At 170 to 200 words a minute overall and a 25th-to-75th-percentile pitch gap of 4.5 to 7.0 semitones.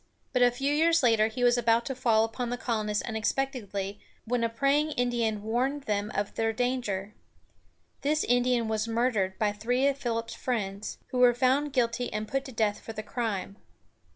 No: average, 180 wpm; average, 2.7 semitones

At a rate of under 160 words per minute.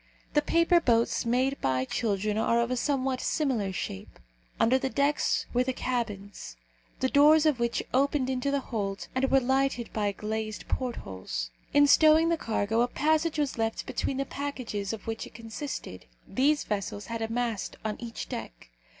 No: average, 175 wpm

